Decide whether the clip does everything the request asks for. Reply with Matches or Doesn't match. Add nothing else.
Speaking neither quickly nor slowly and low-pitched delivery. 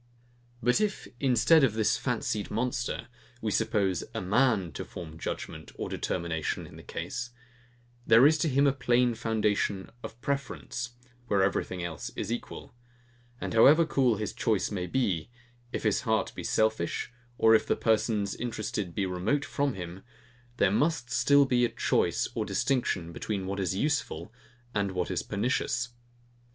Matches